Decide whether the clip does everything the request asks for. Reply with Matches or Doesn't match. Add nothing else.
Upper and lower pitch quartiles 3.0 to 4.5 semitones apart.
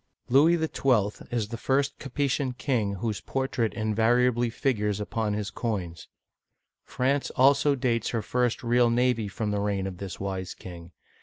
Matches